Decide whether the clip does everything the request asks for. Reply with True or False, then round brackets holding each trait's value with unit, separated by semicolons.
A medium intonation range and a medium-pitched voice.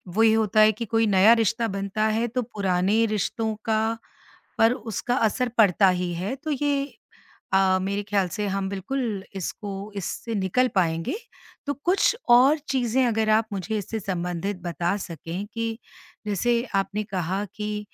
False (3.0 semitones; 210 Hz)